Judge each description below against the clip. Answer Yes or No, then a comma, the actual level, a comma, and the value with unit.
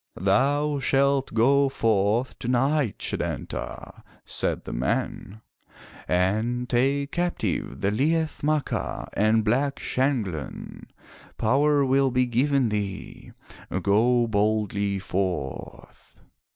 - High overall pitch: No, low, 120 Hz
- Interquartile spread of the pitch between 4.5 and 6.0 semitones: Yes, average, 5.2 semitones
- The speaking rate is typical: No, slow, 95 wpm